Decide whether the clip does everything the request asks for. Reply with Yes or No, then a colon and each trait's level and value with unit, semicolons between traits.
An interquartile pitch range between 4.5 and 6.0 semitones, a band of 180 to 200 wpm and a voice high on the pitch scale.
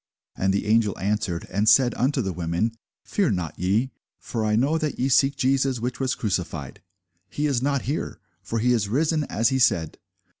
No: average, 5.2 semitones; average, 190 wpm; low, 115 Hz